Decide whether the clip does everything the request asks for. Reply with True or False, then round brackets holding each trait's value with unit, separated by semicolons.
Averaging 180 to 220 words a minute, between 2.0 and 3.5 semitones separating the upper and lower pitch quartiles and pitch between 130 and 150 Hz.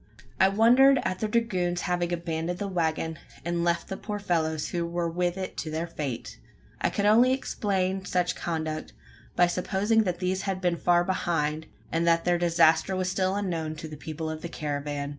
False (190 wpm; 2.8 semitones; 175 Hz)